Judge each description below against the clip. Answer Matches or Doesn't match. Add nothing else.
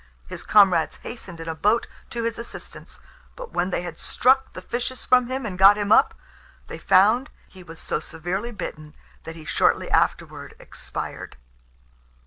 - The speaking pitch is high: Matches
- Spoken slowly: Doesn't match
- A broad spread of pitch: Matches